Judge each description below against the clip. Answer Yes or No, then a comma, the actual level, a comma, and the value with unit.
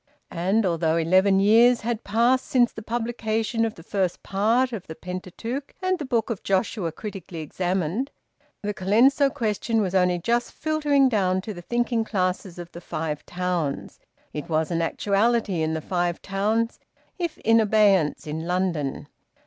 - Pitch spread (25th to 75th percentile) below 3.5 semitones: No, average, 4.6 semitones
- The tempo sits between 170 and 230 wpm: No, average, 160 wpm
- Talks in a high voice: Yes, high, 200 Hz